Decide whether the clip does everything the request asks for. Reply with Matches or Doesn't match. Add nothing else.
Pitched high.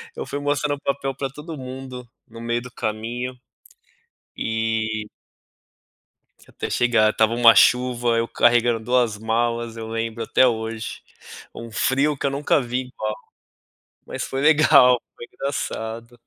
Doesn't match